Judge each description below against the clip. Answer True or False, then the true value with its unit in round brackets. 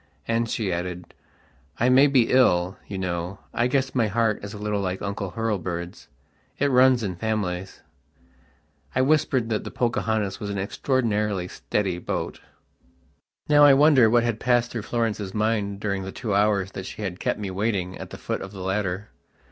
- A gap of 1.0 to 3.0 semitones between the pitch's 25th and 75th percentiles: False (3.7 semitones)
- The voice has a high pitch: False (105 Hz)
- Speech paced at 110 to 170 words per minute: False (180 wpm)